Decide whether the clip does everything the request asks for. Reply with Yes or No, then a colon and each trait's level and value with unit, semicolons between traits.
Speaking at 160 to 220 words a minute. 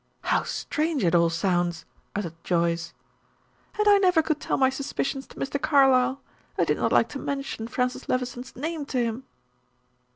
Yes: average, 165 wpm